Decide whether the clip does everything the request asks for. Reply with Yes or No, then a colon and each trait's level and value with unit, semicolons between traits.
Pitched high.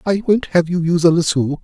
No: medium, 170 Hz